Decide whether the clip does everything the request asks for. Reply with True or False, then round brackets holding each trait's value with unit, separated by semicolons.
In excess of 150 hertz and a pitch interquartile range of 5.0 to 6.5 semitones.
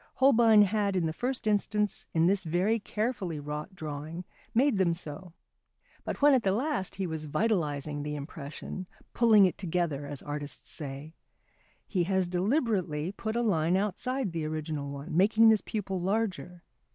True (185 Hz; 5.5 semitones)